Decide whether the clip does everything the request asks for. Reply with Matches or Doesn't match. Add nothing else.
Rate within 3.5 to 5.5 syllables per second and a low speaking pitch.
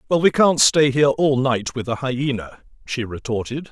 Matches